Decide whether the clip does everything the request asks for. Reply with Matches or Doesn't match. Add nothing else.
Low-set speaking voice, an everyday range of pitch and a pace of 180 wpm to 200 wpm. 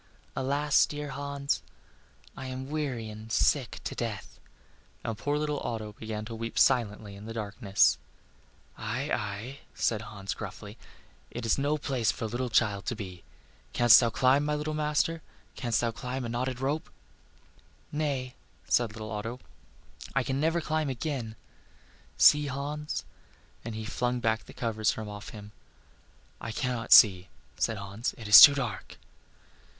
Doesn't match